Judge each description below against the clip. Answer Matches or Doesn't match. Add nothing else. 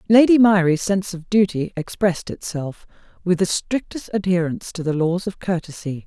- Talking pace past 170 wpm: Doesn't match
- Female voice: Matches